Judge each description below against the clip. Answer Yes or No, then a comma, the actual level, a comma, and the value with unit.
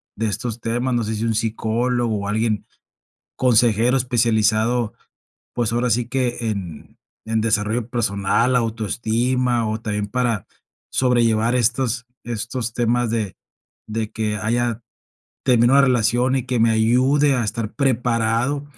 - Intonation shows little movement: Yes, narrow, 2.0 semitones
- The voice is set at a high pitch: No, low, 115 Hz